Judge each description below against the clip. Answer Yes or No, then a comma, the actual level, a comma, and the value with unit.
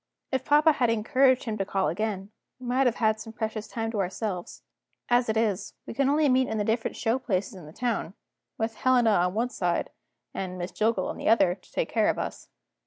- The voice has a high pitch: Yes, high, 225 Hz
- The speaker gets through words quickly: Yes, fast, 225 wpm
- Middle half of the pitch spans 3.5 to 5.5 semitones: Yes, average, 4.0 semitones